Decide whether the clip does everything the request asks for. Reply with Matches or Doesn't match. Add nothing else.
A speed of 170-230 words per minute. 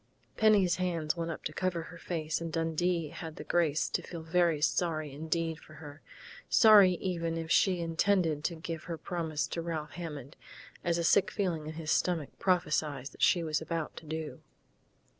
Matches